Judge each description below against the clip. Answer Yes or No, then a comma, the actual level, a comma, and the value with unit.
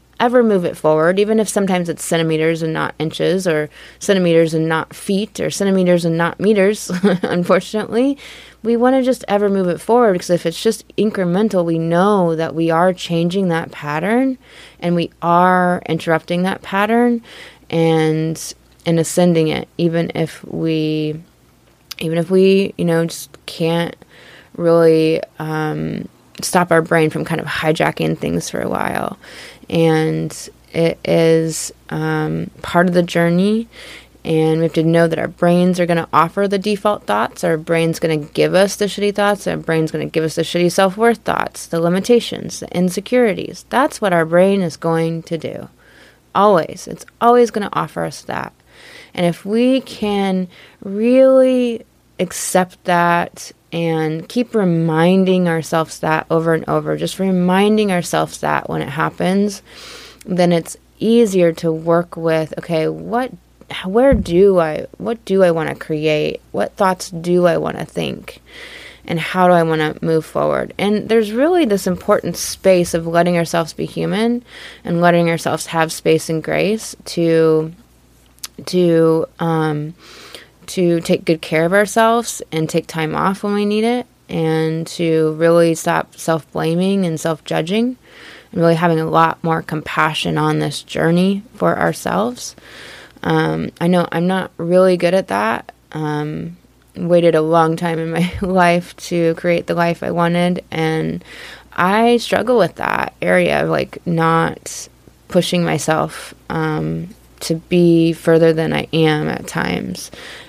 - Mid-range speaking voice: Yes, medium, 170 Hz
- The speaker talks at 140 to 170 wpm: Yes, average, 160 wpm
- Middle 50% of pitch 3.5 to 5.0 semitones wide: No, average, 3.1 semitones